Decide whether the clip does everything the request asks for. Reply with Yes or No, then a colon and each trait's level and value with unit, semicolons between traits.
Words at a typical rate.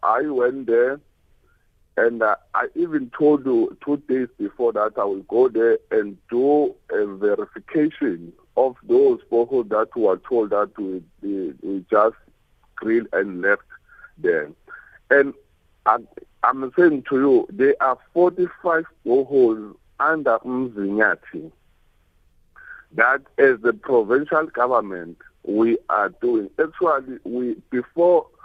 No: slow, 125 wpm